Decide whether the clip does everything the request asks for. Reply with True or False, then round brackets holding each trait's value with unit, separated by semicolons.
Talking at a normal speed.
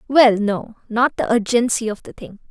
True (190 wpm)